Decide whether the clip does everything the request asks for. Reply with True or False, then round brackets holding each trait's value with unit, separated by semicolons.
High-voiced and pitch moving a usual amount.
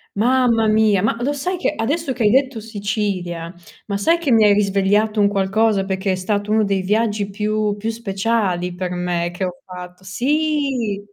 True (210 Hz; 3.0 semitones)